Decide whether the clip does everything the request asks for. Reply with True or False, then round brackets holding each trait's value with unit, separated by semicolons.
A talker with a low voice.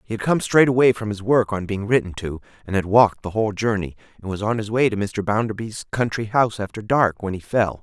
True (110 Hz)